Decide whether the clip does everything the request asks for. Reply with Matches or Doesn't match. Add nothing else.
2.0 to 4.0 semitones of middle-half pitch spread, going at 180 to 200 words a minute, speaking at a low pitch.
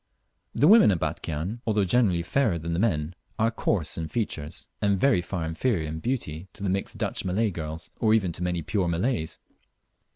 Doesn't match